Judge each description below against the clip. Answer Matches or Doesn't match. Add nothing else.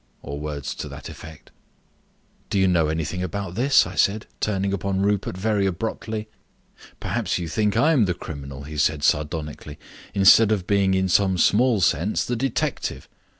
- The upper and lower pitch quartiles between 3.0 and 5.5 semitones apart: Matches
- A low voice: Matches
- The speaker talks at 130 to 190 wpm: Matches